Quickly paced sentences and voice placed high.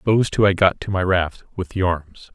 No: fast, 255 wpm; very low, 95 Hz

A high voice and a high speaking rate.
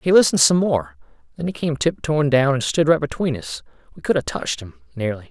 No: medium, 140 Hz; fast, 225 wpm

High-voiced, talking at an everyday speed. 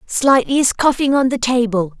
Yes: very high, 250 Hz; average, 180 wpm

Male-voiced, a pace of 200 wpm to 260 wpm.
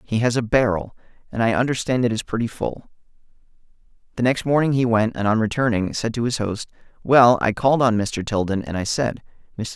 Yes: male; fast, 205 wpm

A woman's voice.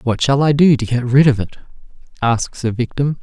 No: male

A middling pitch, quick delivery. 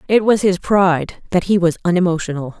No: medium, 180 Hz; average, 185 wpm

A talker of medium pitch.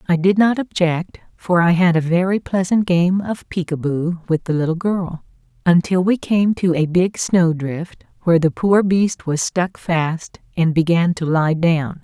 Yes: medium, 175 Hz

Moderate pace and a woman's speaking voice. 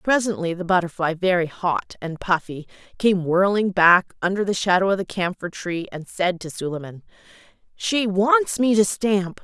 Yes: average, 165 wpm; female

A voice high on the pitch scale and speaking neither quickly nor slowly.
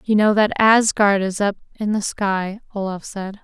Yes: high, 205 Hz; average, 190 wpm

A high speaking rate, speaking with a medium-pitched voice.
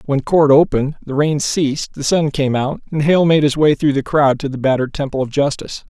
Yes: fast, 240 wpm; medium, 145 Hz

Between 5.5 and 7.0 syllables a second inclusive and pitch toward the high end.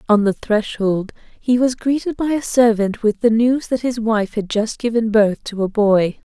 No: 4.5 syllables/s; high, 225 Hz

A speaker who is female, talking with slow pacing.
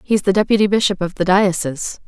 No: female; fast, 205 wpm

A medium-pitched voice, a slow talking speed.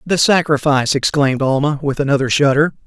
No: medium, 145 Hz; average, 145 wpm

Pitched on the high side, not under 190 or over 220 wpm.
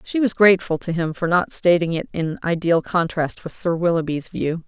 No: medium, 170 Hz; fast, 205 wpm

